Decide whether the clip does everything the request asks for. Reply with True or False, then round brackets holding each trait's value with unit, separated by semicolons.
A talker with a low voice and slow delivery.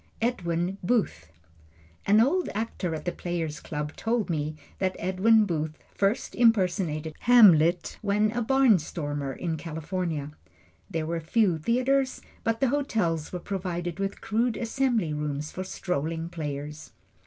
False (180 Hz; 130 wpm)